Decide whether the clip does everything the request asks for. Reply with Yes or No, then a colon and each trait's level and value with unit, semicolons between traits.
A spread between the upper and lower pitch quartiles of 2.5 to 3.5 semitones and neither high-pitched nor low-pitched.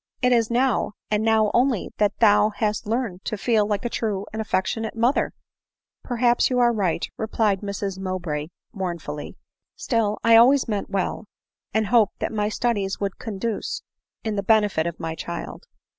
No: average, 2.8 semitones; high, 215 Hz